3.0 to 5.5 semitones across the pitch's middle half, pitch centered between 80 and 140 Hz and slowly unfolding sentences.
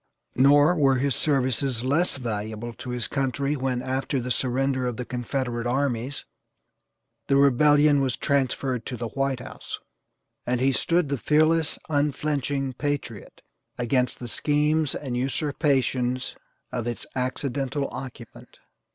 No: narrow, 2.4 semitones; low, 135 Hz; slow, 130 wpm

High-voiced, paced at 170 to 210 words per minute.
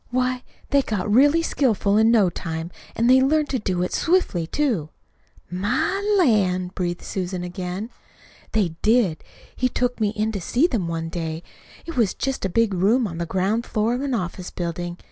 Yes: high, 210 Hz; average, 185 wpm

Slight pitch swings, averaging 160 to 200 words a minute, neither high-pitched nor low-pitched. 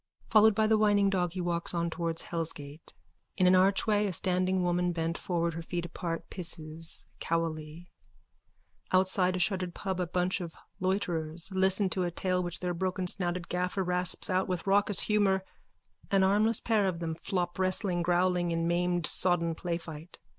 Yes: narrow, 1.9 semitones; average, 165 wpm; medium, 180 Hz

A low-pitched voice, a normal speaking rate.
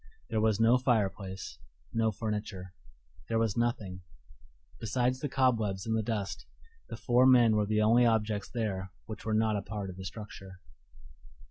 Yes: low, 110 Hz; average, 160 wpm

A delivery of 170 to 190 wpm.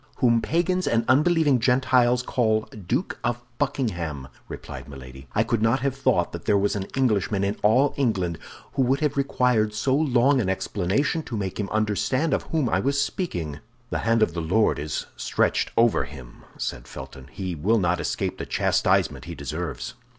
Yes: average, 180 wpm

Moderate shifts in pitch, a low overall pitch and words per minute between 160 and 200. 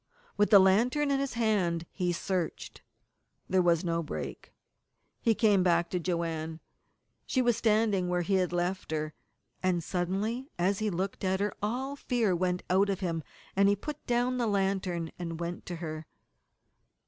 No: average, 3.8 semitones; high, 190 Hz; average, 170 wpm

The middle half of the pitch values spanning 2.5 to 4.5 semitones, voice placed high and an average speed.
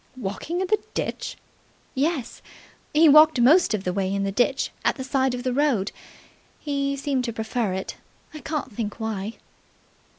No: wide, 5.5 semitones; very high, 255 Hz; average, 170 wpm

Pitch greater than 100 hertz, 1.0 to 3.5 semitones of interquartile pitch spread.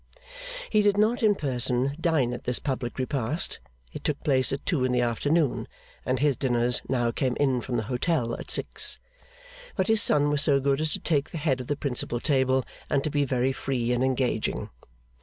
Yes: low, 135 Hz; average, 3.1 semitones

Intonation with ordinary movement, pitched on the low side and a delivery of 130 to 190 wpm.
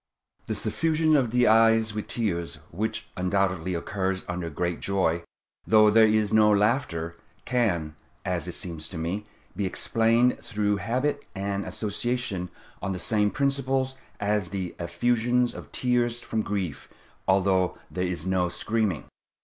Yes: average, 4.3 semitones; low, 105 Hz; average, 140 wpm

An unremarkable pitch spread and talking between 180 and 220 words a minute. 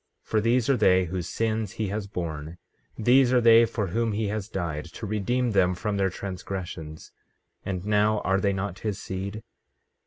Yes: average, 3.0 semitones; average, 185 wpm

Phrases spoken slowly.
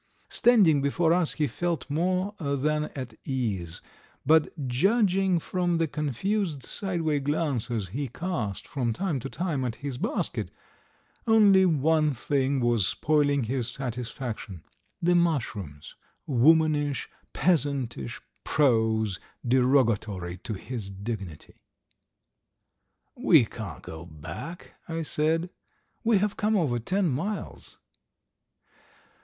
Yes: slow, 110 wpm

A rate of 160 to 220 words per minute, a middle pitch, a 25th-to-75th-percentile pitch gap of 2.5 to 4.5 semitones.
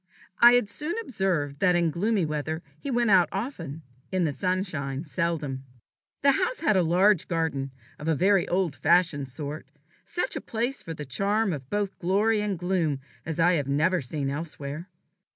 No: average, 175 wpm; medium, 175 Hz; average, 4.9 semitones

